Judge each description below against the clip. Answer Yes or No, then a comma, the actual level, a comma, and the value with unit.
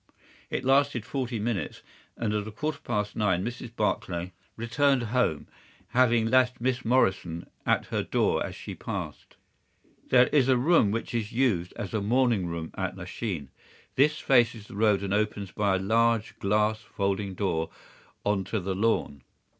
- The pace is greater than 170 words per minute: No, average, 160 wpm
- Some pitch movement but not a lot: Yes, average, 4.0 semitones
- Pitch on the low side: Yes, low, 110 Hz